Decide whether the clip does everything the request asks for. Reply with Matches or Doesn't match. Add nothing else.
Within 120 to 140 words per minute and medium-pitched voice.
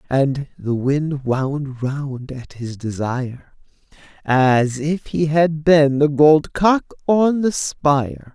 Matches